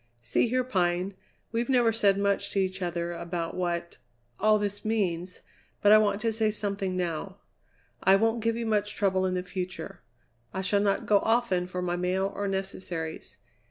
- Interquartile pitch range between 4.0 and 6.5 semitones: No, average, 2.9 semitones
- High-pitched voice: Yes, high, 195 Hz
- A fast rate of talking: No, average, 180 wpm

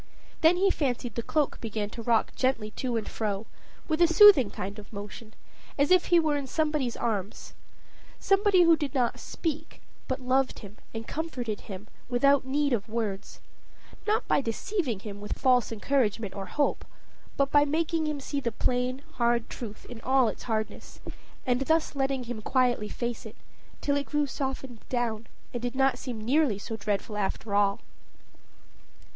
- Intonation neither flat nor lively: Yes, average, 4.6 semitones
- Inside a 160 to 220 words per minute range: Yes, average, 170 wpm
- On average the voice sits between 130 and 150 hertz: No, very high, 250 Hz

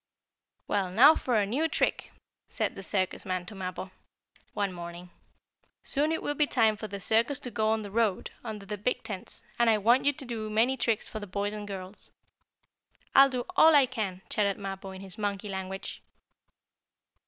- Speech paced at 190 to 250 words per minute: Yes, average, 195 wpm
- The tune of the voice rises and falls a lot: No, average, 3.7 semitones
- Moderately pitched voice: No, high, 210 Hz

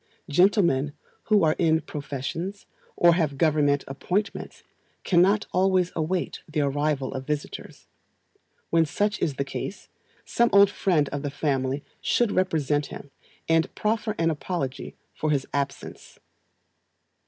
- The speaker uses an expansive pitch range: No, average, 4.6 semitones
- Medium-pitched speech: Yes, medium, 160 Hz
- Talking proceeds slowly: Yes, slow, 130 wpm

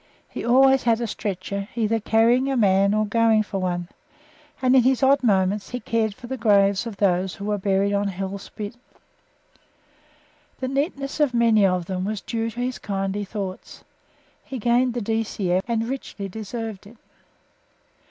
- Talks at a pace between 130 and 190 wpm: Yes, average, 170 wpm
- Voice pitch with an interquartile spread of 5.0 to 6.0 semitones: No, average, 3.4 semitones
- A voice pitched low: No, high, 215 Hz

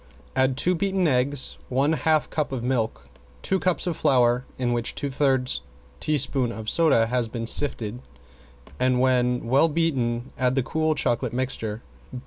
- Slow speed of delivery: No, average, 155 wpm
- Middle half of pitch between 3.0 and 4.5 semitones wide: Yes, average, 3.5 semitones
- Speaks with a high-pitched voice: No, low, 130 Hz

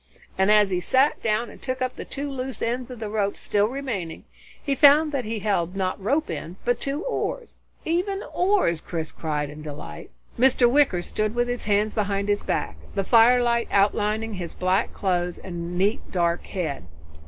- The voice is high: Yes, high, 210 Hz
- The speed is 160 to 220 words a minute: Yes, average, 180 wpm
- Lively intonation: Yes, wide, 5.8 semitones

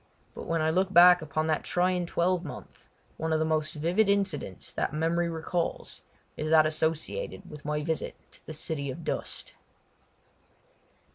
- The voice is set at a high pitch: No, medium, 160 Hz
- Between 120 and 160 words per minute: Yes, average, 155 wpm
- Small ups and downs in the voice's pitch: Yes, narrow, 2.3 semitones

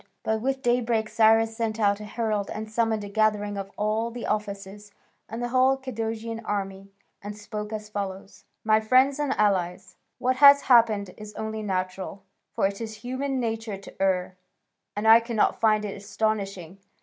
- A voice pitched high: Yes, high, 215 Hz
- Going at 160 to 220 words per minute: Yes, average, 170 wpm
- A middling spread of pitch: No, narrow, 2.2 semitones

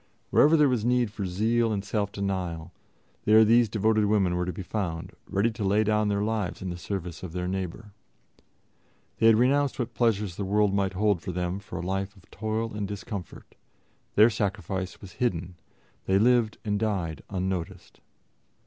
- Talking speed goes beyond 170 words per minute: Yes, average, 180 wpm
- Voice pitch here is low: Yes, low, 100 Hz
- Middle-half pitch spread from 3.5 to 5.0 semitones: No, average, 3.0 semitones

